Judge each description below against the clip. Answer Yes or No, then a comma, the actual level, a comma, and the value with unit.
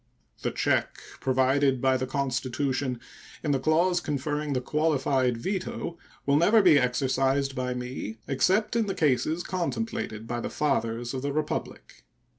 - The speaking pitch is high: No, medium, 140 Hz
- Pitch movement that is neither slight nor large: Yes, average, 3.4 semitones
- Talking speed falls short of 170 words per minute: Yes, average, 145 wpm